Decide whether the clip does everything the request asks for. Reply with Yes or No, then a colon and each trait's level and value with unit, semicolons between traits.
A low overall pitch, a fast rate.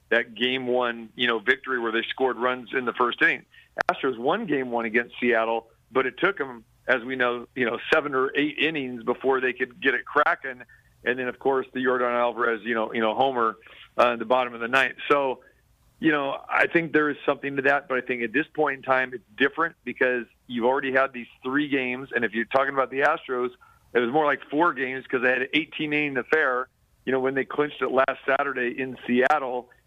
Yes: low, 125 Hz; fast, 230 wpm